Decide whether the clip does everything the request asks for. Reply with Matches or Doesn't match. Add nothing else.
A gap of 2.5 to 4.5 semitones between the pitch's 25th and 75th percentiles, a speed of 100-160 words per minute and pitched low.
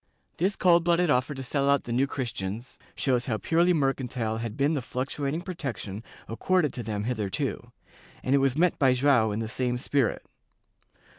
Doesn't match